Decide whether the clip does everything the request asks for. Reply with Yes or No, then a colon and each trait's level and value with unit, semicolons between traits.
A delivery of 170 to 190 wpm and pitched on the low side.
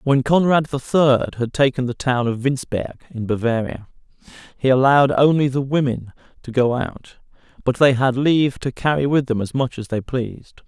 Yes: average, 185 wpm; low, 130 Hz